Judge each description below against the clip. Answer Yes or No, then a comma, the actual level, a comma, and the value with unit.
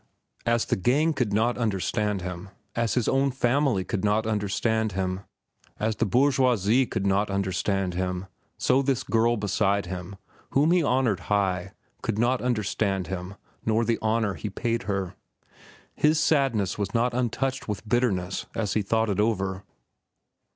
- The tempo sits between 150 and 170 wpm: Yes, average, 155 wpm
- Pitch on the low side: Yes, low, 110 Hz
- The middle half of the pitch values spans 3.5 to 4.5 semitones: Yes, average, 3.9 semitones